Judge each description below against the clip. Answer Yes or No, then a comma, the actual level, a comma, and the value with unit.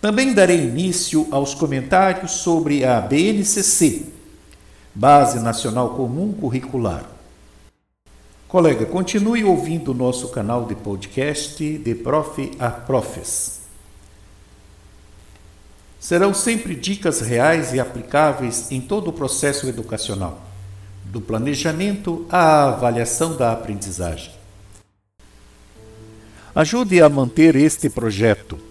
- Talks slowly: Yes, slow, 95 wpm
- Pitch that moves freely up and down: Yes, wide, 8.0 semitones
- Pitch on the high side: No, low, 125 Hz